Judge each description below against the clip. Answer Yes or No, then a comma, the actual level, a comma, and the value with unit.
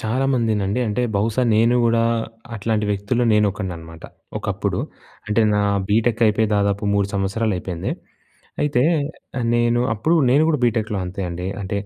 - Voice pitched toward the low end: Yes, low, 110 Hz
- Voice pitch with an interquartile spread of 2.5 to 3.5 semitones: Yes, average, 2.9 semitones